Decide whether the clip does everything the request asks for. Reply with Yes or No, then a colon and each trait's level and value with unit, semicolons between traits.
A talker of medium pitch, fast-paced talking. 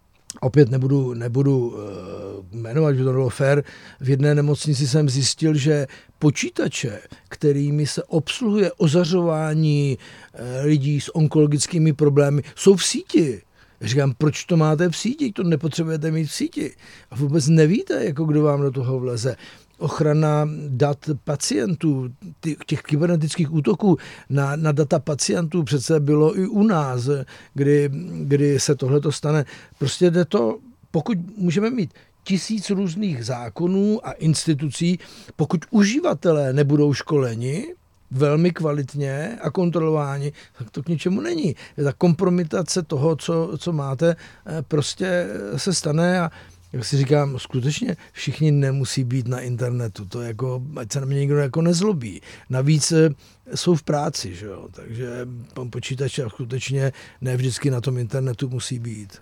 No: medium, 145 Hz; average, 140 wpm